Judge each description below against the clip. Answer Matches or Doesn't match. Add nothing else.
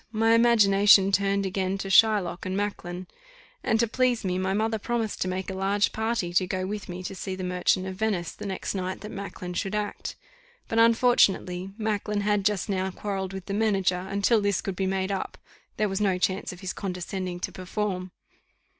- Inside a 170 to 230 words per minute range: Matches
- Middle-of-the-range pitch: Doesn't match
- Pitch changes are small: Matches